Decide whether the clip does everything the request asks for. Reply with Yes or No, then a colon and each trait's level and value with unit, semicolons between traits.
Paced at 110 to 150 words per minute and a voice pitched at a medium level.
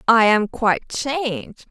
No: average, 140 wpm; high, 230 Hz